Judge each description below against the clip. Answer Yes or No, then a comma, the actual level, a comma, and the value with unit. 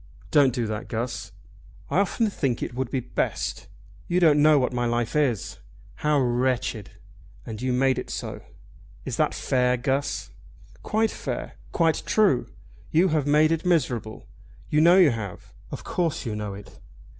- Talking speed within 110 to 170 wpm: Yes, average, 165 wpm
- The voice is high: No, low, 130 Hz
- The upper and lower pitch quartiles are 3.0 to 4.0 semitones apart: No, average, 4.6 semitones